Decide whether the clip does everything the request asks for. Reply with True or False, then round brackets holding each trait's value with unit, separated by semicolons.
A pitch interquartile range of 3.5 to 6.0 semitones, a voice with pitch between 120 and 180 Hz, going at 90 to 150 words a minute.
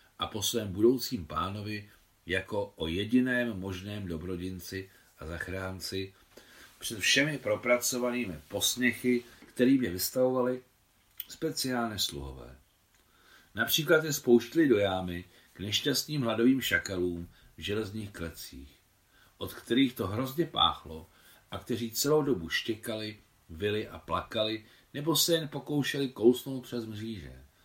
False (5.1 semitones; 105 Hz; 115 wpm)